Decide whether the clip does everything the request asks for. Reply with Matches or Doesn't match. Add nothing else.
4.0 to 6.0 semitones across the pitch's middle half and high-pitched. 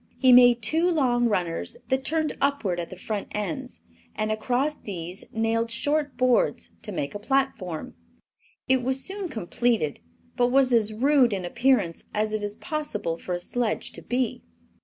Matches